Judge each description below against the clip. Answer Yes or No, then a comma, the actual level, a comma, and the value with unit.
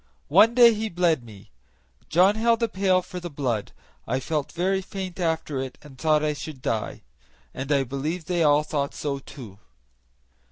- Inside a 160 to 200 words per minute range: Yes, average, 175 wpm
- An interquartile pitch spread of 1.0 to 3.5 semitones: No, average, 5.1 semitones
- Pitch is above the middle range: No, medium, 155 Hz